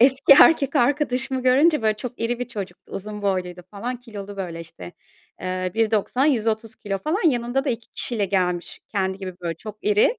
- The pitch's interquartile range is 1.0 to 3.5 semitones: No, average, 4.6 semitones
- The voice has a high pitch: Yes, high, 220 Hz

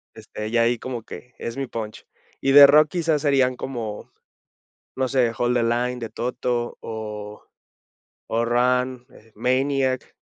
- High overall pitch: No, low, 125 Hz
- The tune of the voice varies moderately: No, narrow, 2.2 semitones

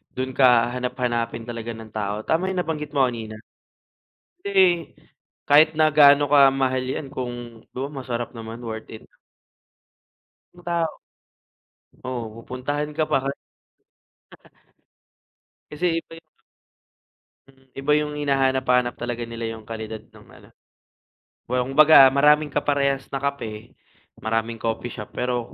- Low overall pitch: Yes, low, 130 Hz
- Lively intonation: No, average, 3.8 semitones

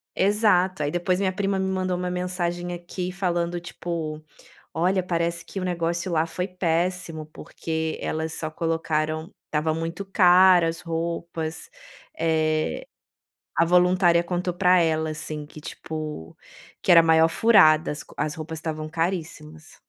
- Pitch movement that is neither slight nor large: No, narrow, 2.3 semitones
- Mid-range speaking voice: Yes, medium, 170 Hz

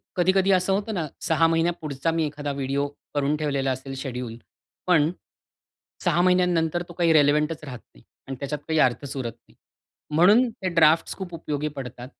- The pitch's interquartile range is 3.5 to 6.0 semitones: Yes, average, 3.9 semitones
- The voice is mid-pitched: Yes, medium, 155 Hz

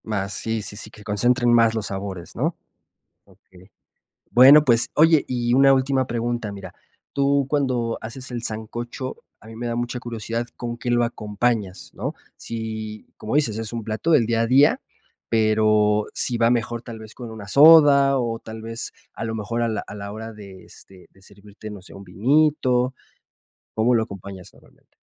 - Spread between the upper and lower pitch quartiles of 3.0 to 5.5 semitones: No, narrow, 2.5 semitones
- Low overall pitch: Yes, low, 115 Hz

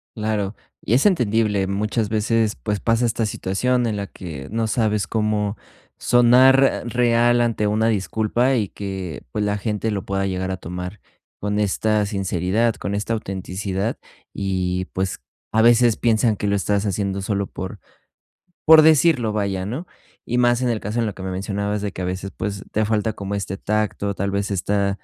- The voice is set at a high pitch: No, low, 105 Hz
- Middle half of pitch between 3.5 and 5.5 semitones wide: No, narrow, 2.6 semitones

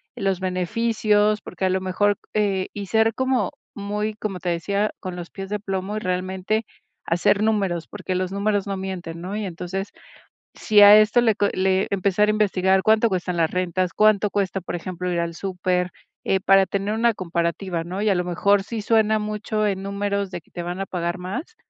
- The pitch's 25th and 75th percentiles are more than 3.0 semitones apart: No, narrow, 2.5 semitones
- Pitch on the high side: Yes, high, 195 Hz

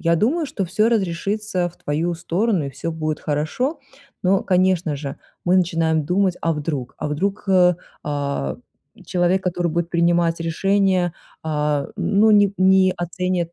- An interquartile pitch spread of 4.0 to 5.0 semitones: No, average, 3.0 semitones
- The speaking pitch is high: No, medium, 175 Hz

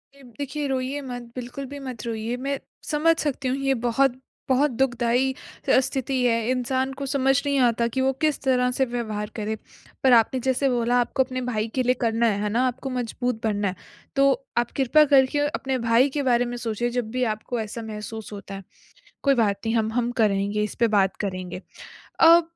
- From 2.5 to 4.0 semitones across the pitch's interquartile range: Yes, average, 3.1 semitones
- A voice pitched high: Yes, very high, 250 Hz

